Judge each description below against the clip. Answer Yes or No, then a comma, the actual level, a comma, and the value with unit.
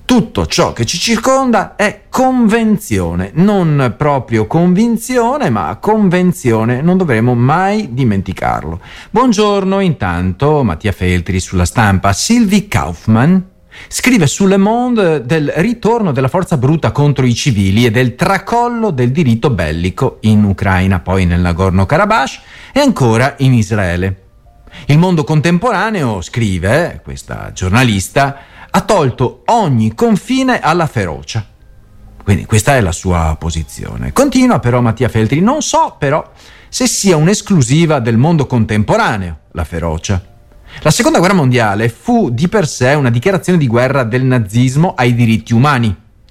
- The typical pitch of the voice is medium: No, low, 125 Hz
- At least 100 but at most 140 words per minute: Yes, average, 130 wpm